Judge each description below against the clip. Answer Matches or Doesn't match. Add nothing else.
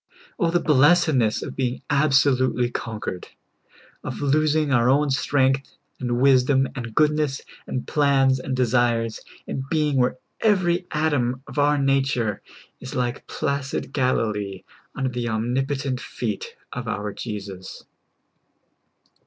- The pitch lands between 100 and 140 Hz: Matches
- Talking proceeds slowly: Matches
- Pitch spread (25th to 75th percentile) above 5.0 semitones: Doesn't match